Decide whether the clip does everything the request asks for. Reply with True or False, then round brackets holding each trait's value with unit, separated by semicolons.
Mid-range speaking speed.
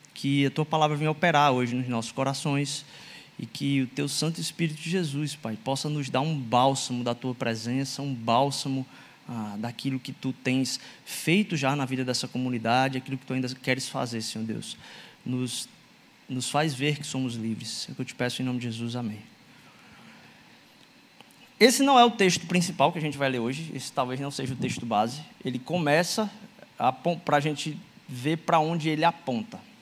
False (195 wpm)